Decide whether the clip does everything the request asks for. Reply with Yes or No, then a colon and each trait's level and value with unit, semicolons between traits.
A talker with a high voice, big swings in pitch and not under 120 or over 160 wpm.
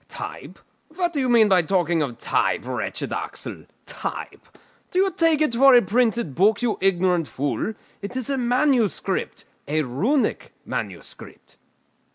Yes: high, 225 Hz; wide, 6.9 semitones; average, 150 wpm